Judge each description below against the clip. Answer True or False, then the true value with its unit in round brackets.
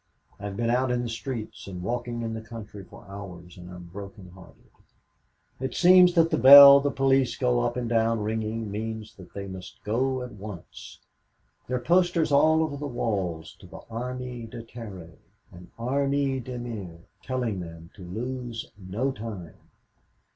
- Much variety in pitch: False (4.5 semitones)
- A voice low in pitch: True (115 Hz)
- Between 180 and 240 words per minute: False (170 wpm)